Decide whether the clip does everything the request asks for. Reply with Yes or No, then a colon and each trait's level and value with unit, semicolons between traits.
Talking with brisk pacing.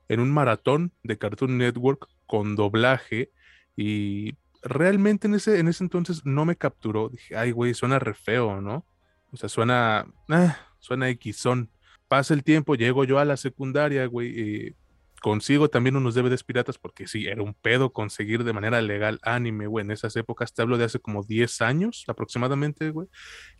No: average, 175 wpm